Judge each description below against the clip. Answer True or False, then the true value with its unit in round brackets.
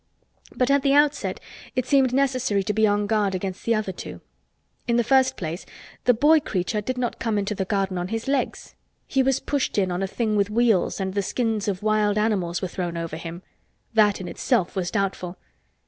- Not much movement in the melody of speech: False (4.7 semitones)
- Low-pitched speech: False (210 Hz)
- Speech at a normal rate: False (210 wpm)